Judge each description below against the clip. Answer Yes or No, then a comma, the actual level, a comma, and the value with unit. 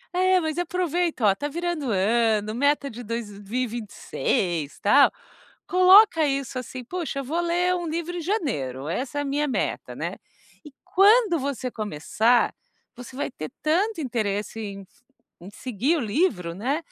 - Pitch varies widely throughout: Yes, wide, 7.9 semitones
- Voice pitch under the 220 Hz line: No, very high, 275 Hz